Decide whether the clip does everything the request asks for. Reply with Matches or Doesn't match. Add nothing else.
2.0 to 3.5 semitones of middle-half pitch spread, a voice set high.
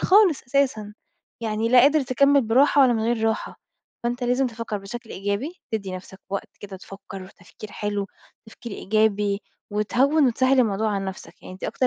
Doesn't match